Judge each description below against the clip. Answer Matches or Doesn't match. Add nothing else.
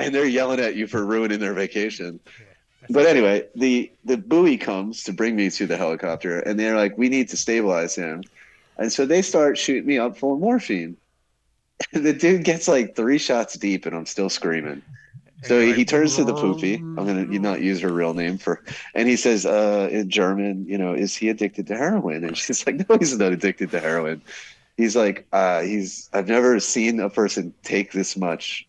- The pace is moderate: Doesn't match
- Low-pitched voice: Matches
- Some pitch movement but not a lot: Matches